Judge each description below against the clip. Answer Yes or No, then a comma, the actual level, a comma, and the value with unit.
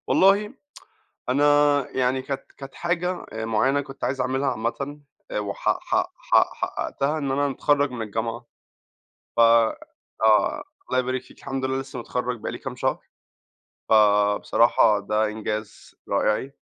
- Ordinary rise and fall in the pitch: Yes, average, 3.9 semitones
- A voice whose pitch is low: Yes, low, 130 Hz